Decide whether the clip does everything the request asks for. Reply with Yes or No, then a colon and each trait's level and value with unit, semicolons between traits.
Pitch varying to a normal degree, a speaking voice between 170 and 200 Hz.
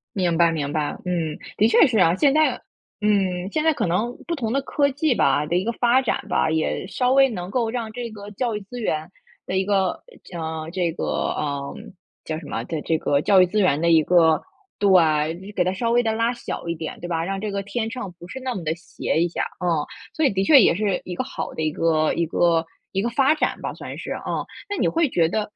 No: wide, 6.1 semitones; high, 190 Hz